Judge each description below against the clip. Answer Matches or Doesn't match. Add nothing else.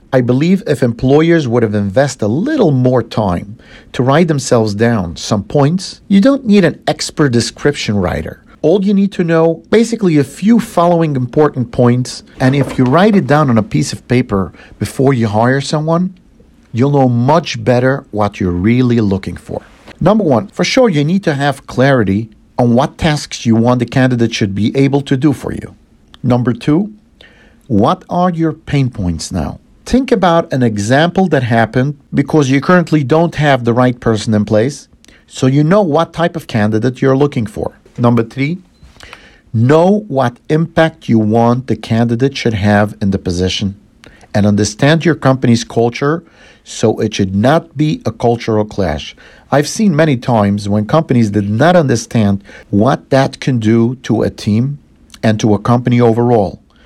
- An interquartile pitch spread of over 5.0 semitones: Matches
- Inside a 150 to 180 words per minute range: Matches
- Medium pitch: Doesn't match